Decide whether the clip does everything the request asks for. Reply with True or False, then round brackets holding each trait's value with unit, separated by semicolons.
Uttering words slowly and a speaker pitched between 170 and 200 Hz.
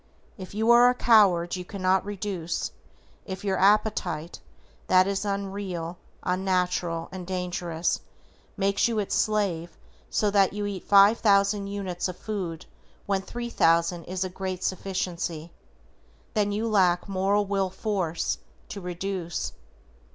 True (130 wpm; 190 Hz)